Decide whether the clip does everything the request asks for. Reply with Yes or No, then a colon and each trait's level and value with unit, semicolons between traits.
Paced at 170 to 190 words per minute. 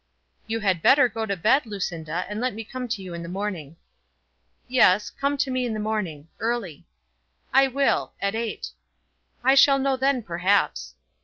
Yes: average, 175 wpm